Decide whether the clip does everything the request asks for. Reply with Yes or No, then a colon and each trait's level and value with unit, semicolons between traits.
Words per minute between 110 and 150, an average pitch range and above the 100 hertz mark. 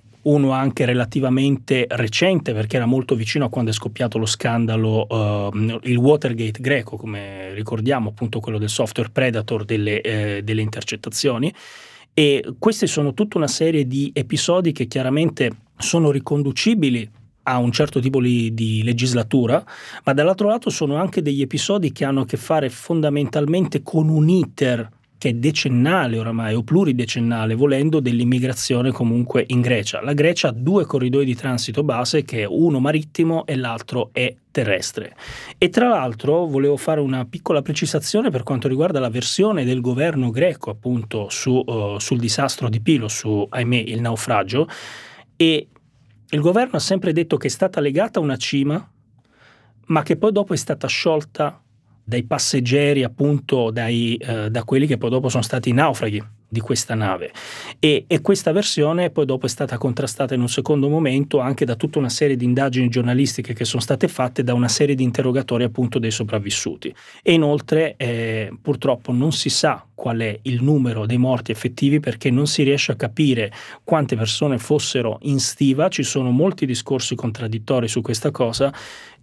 No: average, 165 wpm; average, 3.9 semitones; low, 130 Hz